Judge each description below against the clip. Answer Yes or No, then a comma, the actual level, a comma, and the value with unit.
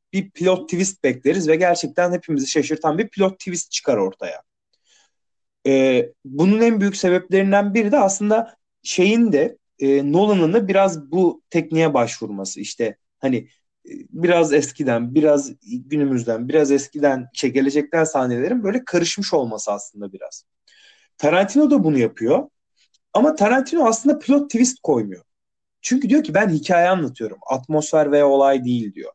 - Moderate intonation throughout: No, wide, 6.3 semitones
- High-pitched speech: No, medium, 170 Hz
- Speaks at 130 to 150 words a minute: Yes, fast, 140 wpm